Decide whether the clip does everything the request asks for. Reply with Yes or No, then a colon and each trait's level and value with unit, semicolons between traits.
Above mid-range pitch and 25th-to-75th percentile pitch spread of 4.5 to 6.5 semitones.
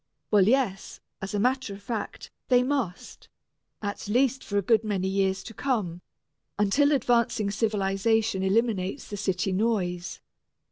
No: high, 210 Hz; average, 3.5 semitones